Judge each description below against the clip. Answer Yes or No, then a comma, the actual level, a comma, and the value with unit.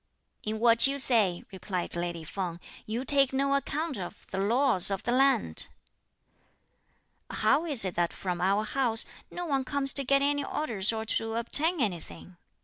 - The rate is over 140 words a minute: Yes, average, 165 wpm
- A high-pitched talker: Yes, high, 230 Hz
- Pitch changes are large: Yes, wide, 6.3 semitones